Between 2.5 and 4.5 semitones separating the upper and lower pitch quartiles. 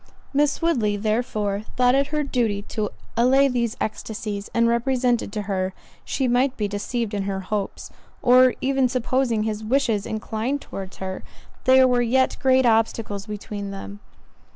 Yes: average, 3.8 semitones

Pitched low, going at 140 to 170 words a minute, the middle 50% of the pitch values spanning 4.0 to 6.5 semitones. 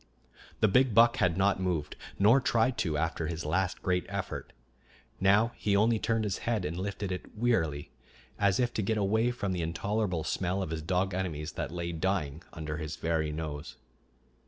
No: very low, 95 Hz; average, 180 wpm; average, 4.5 semitones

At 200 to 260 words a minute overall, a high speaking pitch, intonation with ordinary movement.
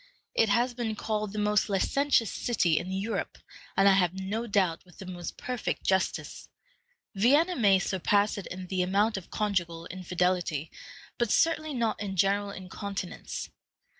No: average, 155 wpm; high, 200 Hz; average, 3.0 semitones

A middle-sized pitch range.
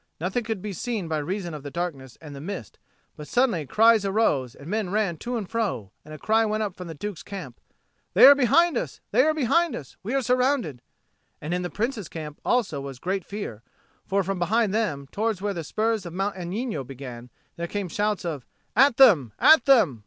No: wide, 6.4 semitones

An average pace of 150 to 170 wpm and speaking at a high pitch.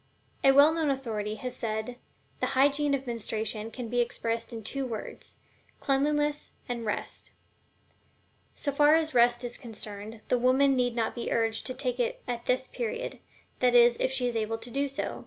No: average, 185 wpm; high, 245 Hz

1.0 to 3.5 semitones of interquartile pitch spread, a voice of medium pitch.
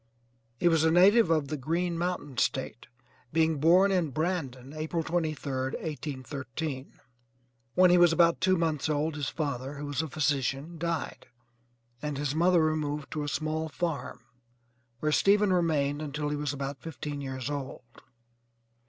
Yes: average, 2.9 semitones; medium, 155 Hz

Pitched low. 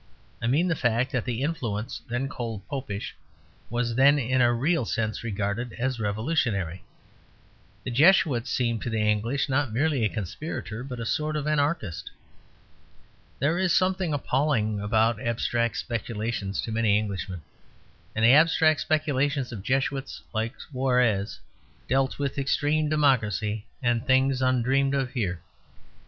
Yes: low, 125 Hz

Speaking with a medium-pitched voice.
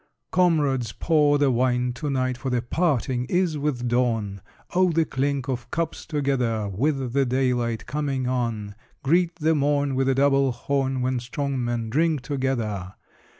No: low, 130 Hz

